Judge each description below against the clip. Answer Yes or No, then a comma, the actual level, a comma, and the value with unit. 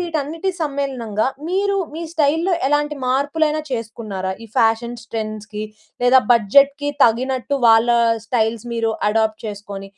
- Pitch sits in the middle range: No, high, 240 Hz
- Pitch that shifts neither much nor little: Yes, average, 4.9 semitones